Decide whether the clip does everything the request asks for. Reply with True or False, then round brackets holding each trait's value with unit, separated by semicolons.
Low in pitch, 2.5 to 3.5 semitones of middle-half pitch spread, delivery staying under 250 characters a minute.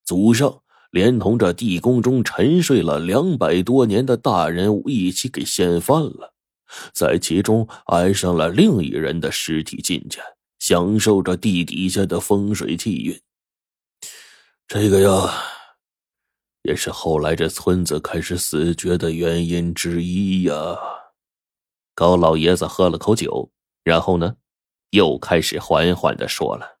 True (90 Hz; 3.2 semitones; 200 characters per minute)